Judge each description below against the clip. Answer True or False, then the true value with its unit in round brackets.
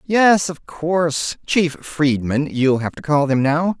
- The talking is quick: False (160 wpm)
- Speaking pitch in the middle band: True (155 Hz)